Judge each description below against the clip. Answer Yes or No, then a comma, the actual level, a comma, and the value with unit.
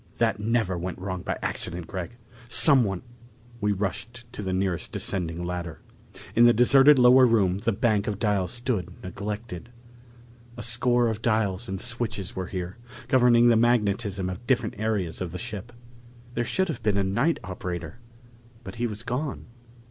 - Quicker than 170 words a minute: No, average, 165 wpm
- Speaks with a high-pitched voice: No, low, 105 Hz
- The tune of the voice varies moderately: Yes, average, 4.3 semitones